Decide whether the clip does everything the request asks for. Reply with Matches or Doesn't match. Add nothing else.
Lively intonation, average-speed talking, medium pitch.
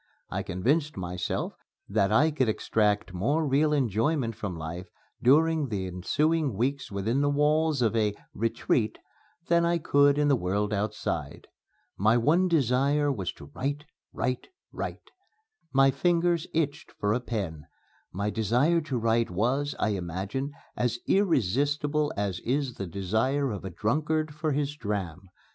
Doesn't match